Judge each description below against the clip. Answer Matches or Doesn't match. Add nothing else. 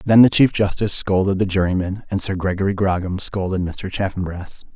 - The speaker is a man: Matches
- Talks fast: Doesn't match